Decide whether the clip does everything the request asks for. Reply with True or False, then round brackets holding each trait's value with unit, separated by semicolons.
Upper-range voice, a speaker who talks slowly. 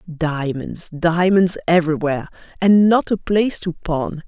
False (170 Hz; 125 wpm)